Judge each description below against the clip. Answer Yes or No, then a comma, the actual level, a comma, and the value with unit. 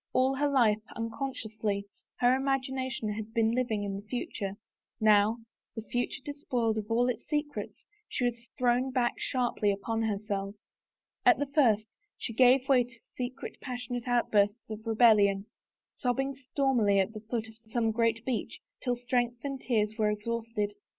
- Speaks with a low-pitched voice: No, high, 235 Hz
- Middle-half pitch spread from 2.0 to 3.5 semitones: Yes, average, 2.9 semitones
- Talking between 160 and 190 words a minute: No, average, 150 wpm